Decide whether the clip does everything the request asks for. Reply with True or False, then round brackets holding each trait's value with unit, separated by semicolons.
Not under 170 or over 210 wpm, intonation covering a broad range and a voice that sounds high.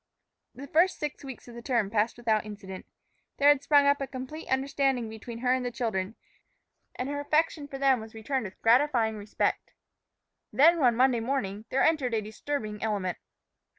False (180 wpm; 4.2 semitones; 250 Hz)